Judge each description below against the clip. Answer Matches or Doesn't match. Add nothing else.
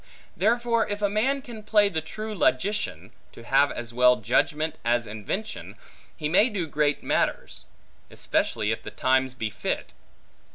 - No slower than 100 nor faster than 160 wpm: Matches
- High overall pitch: Doesn't match